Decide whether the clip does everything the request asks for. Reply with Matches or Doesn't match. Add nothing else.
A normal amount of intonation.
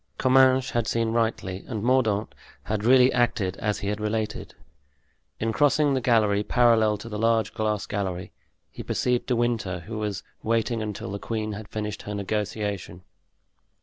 Doesn't match